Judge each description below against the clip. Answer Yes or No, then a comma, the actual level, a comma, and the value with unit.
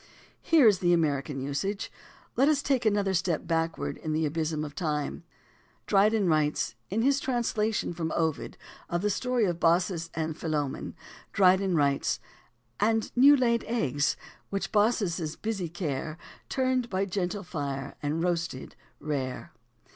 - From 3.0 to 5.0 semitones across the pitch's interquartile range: No, wide, 5.5 semitones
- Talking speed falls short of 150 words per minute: Yes, average, 140 wpm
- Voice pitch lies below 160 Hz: No, medium, 175 Hz